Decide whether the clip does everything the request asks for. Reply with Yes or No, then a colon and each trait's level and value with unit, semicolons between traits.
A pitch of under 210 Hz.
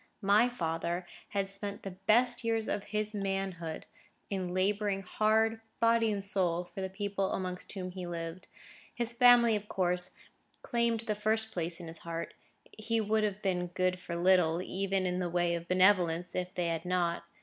Yes: high, 190 Hz